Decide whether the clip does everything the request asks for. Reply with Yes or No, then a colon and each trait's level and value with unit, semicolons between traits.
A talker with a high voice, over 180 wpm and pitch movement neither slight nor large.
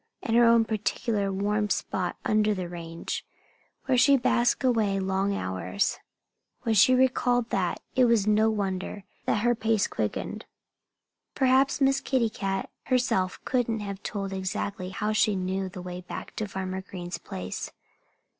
No: high, 205 Hz; average, 150 wpm; average, 3.6 semitones